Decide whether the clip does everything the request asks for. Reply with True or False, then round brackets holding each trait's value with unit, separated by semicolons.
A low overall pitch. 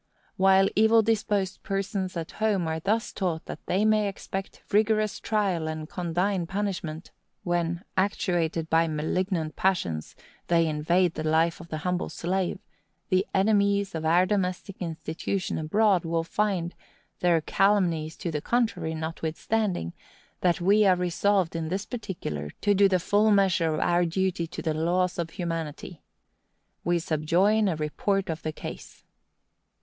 False (180 Hz)